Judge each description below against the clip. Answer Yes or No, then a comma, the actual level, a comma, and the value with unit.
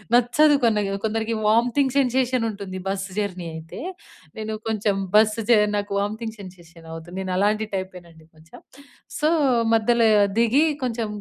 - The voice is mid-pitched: No, high, 215 Hz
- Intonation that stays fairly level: No, average, 3.9 semitones